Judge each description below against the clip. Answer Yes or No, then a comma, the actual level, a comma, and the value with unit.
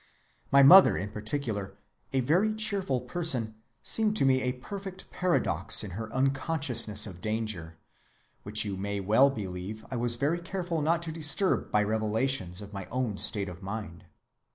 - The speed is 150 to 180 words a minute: Yes, average, 160 wpm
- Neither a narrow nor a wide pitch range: No, wide, 7.4 semitones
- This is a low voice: Yes, low, 120 Hz